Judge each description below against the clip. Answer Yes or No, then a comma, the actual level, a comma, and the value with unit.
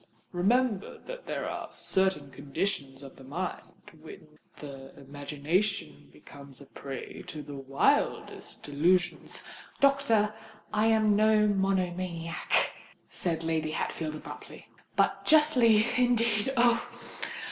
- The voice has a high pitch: No, medium, 180 Hz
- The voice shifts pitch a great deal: Yes, wide, 7.0 semitones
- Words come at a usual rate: No, slow, 105 wpm